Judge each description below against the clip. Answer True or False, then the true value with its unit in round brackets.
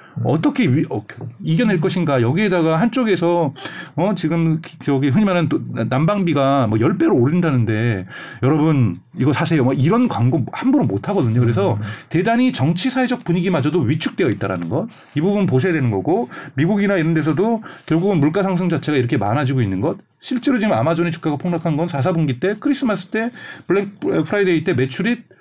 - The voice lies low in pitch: False (165 Hz)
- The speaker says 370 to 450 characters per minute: True (385 characters per minute)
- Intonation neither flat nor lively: False (5.9 semitones)